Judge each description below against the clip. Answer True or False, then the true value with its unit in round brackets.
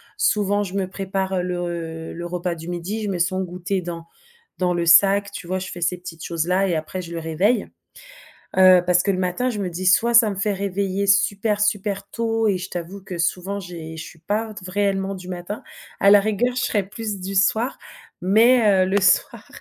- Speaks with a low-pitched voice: False (190 Hz)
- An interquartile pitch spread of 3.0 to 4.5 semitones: False (2.4 semitones)